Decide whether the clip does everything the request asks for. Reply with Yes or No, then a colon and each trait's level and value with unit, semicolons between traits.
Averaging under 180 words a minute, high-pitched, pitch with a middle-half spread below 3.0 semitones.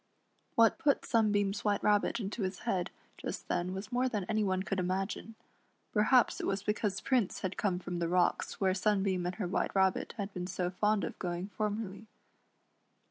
No: average, 185 wpm; high, 195 Hz; narrow, 2.4 semitones